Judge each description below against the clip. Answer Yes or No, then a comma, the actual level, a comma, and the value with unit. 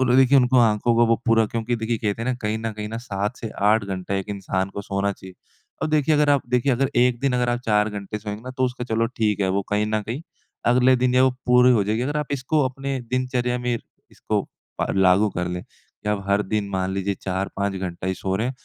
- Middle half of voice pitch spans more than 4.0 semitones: No, average, 3.7 semitones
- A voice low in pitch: Yes, low, 110 Hz